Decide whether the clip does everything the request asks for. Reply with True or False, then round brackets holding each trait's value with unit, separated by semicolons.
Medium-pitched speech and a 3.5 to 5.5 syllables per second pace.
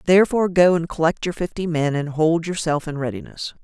False (165 Hz; 5.9 syllables/s)